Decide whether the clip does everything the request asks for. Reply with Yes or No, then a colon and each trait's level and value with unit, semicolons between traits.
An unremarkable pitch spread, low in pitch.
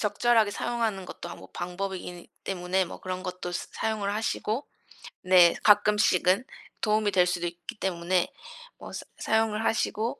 No: average, 3.3 semitones; high, 195 Hz